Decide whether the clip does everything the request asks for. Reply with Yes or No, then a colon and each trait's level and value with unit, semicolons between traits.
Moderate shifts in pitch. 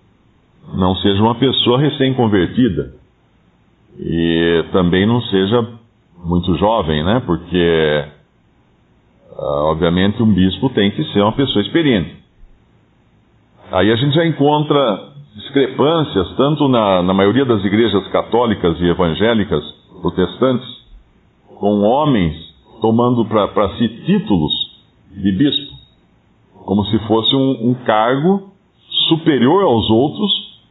No: wide, 6.5 semitones